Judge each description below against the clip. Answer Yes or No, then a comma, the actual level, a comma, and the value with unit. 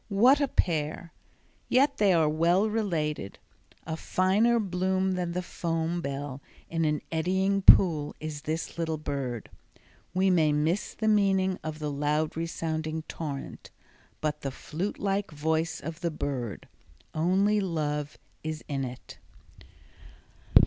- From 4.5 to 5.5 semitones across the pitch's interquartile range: No, average, 3.8 semitones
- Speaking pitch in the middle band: Yes, medium, 165 Hz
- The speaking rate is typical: No, slow, 130 wpm